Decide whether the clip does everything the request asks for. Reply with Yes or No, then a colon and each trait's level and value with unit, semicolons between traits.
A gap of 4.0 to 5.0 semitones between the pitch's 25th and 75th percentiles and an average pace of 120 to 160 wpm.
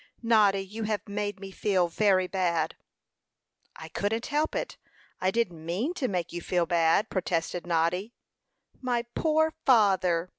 Yes: average, 4.3 semitones; average, 145 wpm